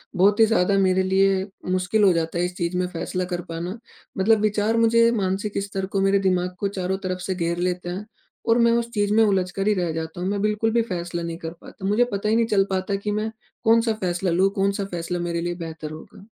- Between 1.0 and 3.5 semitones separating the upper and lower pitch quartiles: Yes, average, 2.8 semitones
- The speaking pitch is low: No, high, 190 Hz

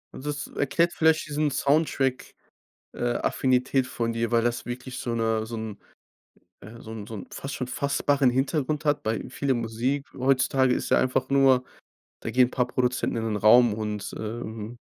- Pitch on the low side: Yes, low, 125 Hz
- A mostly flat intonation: No, average, 3.1 semitones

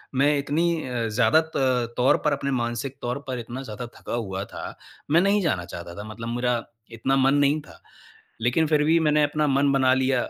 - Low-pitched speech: Yes, low, 130 Hz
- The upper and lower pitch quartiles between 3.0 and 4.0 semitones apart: Yes, average, 3.6 semitones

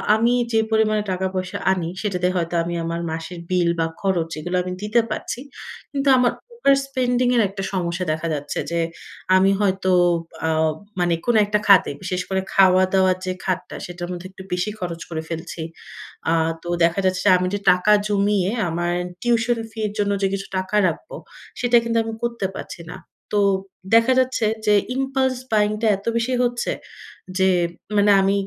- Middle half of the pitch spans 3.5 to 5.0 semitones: Yes, average, 3.8 semitones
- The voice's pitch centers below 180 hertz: No, high, 190 Hz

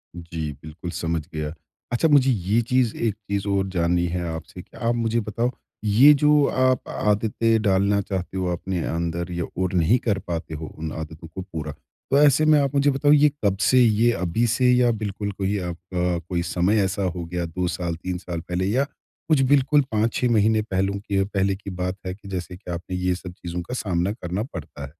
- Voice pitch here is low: Yes, very low, 95 Hz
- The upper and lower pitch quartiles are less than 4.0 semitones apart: No, average, 4.7 semitones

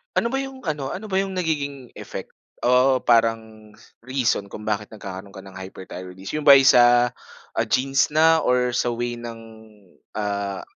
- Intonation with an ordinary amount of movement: Yes, average, 5.0 semitones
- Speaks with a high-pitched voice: No, low, 120 Hz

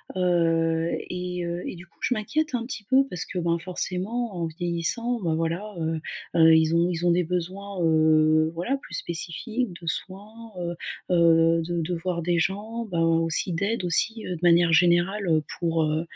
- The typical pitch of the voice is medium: Yes, medium, 175 Hz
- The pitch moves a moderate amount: Yes, average, 3.2 semitones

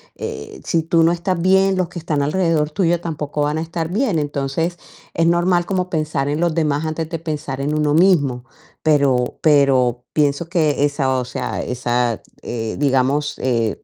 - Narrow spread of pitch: No, average, 3.4 semitones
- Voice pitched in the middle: Yes, medium, 150 Hz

